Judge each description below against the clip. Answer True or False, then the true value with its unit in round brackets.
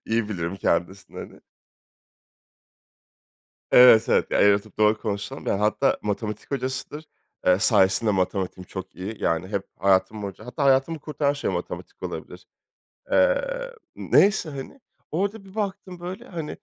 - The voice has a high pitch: False (110 Hz)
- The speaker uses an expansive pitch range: True (8.2 semitones)